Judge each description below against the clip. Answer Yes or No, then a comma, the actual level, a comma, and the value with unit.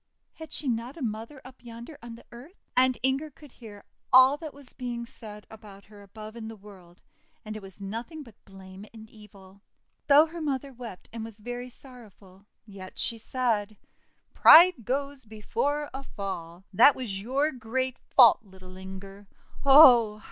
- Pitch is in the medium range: No, high, 230 Hz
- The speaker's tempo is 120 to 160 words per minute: No, average, 175 wpm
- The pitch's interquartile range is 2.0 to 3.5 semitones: No, average, 4.3 semitones